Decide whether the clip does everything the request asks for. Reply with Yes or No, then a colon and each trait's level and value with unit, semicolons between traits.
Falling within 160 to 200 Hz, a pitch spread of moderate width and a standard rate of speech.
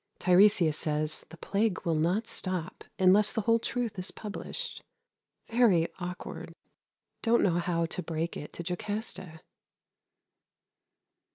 No: medium, 185 Hz; average, 4.0 semitones; slow, 120 wpm